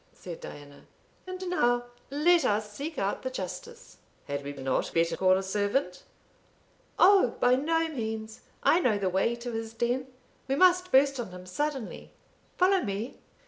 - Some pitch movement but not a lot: No, wide, 8.5 semitones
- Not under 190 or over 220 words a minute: No, average, 160 wpm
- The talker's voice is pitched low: No, high, 240 Hz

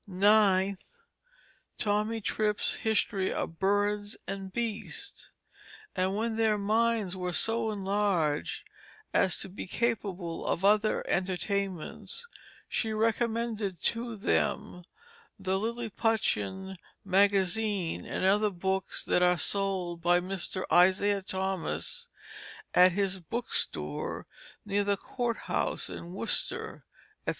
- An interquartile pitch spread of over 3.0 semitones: No, narrow, 2.6 semitones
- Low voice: No, high, 200 Hz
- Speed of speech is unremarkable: No, slow, 110 wpm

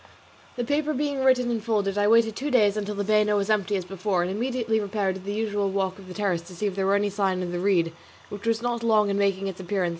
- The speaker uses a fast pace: Yes, fast, 270 wpm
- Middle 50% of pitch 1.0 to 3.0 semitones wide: Yes, narrow, 2.6 semitones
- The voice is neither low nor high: No, high, 205 Hz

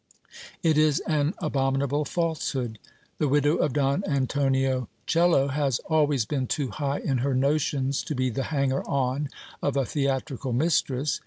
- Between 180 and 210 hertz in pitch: No, medium, 140 Hz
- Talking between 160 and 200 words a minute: No, average, 150 wpm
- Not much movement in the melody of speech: Yes, narrow, 2.1 semitones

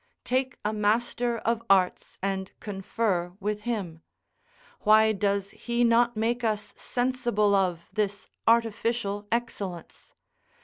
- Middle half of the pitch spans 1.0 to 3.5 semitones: Yes, average, 2.9 semitones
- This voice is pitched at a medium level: No, high, 215 Hz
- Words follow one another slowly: Yes, slow, 115 wpm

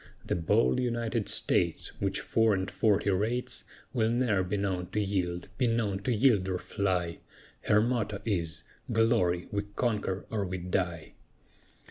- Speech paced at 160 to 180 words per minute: No, average, 150 wpm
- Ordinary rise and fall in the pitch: Yes, average, 3.6 semitones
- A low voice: Yes, low, 100 Hz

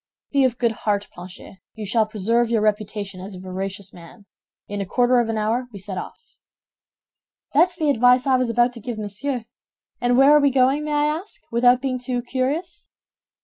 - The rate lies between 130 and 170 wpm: No, average, 195 wpm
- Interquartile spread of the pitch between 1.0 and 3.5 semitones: No, average, 4.1 semitones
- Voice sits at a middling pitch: No, high, 240 Hz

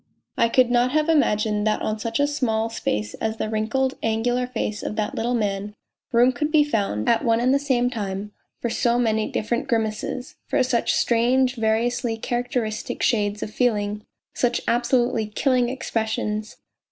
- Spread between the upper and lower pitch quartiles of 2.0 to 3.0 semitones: Yes, narrow, 2.6 semitones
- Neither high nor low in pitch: No, high, 230 Hz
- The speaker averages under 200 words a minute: Yes, average, 165 wpm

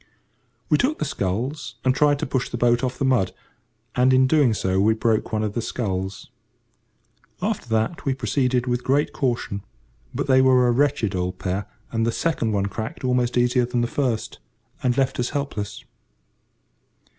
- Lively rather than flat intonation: No, average, 3.3 semitones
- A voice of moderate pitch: No, low, 125 Hz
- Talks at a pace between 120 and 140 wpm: No, average, 180 wpm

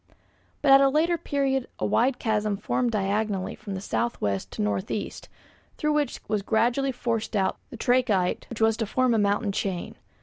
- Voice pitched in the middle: No, high, 225 Hz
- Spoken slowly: No, average, 180 wpm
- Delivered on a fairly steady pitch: No, average, 4.2 semitones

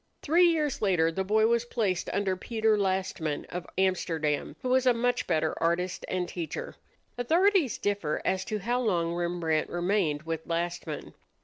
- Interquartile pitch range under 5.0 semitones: No, wide, 5.5 semitones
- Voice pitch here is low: No, high, 190 Hz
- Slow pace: No, average, 155 wpm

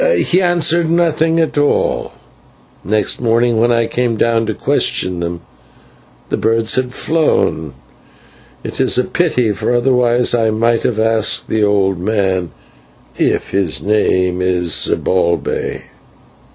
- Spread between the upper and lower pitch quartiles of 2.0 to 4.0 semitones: No, average, 4.4 semitones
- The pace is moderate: No, slow, 125 wpm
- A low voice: Yes, low, 115 Hz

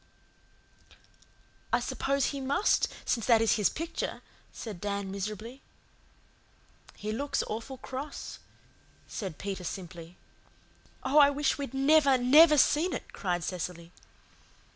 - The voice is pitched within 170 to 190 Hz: No, high, 240 Hz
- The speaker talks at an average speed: No, slow, 120 wpm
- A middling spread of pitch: No, wide, 6.2 semitones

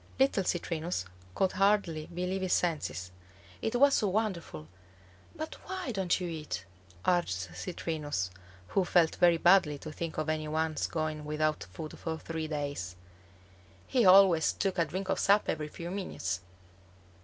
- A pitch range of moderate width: Yes, average, 3.8 semitones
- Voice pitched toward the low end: No, medium, 165 Hz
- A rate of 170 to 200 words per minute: No, average, 150 wpm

